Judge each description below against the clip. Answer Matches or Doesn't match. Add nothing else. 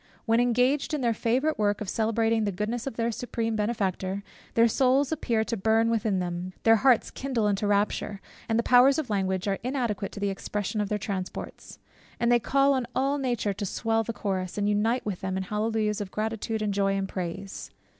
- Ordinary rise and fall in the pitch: Matches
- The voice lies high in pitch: Matches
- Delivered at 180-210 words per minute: Matches